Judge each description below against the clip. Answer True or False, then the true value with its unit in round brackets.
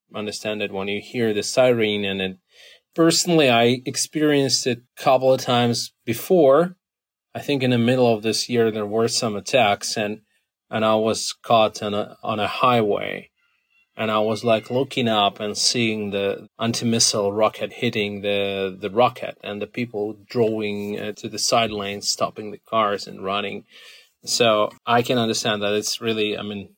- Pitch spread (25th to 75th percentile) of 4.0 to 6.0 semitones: False (2.8 semitones)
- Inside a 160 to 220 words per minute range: True (175 wpm)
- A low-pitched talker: True (110 Hz)